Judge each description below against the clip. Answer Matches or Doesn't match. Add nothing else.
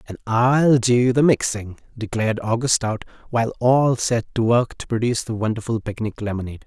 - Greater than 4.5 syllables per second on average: Matches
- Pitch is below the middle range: Matches